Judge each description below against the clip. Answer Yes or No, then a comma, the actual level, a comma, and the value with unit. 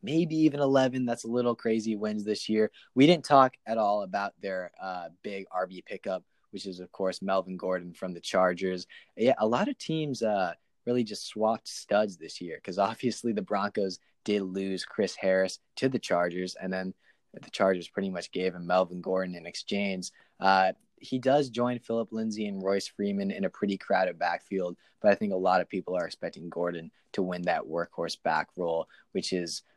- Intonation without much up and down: No, average, 4.0 semitones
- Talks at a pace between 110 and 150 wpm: No, average, 195 wpm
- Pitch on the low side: Yes, low, 100 Hz